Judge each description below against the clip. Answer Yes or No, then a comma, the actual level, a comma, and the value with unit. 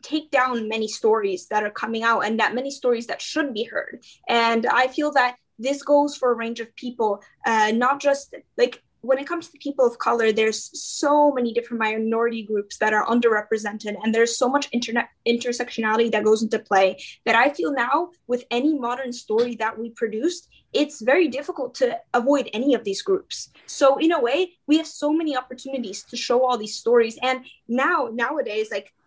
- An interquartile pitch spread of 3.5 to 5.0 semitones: Yes, average, 4.1 semitones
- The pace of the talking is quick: No, average, 195 wpm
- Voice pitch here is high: Yes, high, 245 Hz